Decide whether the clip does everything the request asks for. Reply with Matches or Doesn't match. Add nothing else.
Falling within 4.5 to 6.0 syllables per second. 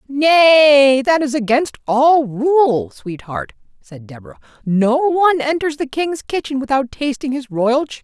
Doesn't match